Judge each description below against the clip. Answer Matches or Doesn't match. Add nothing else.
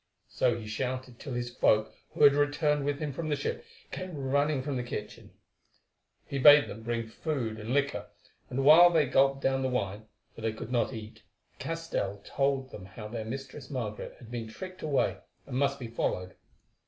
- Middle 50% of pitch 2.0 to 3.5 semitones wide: Doesn't match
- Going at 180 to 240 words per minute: Matches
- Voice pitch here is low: Matches